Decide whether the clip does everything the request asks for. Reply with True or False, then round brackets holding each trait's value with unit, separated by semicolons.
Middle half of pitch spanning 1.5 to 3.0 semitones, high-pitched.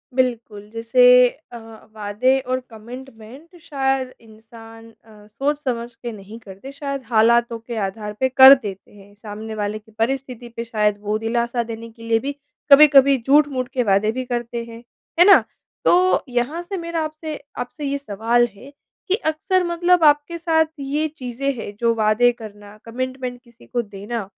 False (3.8 semitones; 240 Hz)